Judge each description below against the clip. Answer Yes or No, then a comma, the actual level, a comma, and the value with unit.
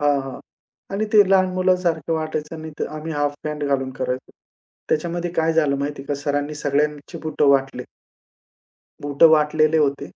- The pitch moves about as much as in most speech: No, narrow, 2.2 semitones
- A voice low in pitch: No, medium, 150 Hz